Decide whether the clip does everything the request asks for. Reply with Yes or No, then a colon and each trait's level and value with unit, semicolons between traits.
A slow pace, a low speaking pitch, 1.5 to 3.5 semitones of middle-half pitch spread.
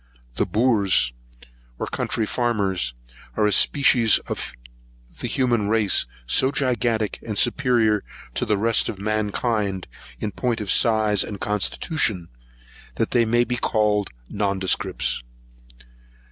Yes: slow, 120 wpm; low, 110 Hz; average, 2.9 semitones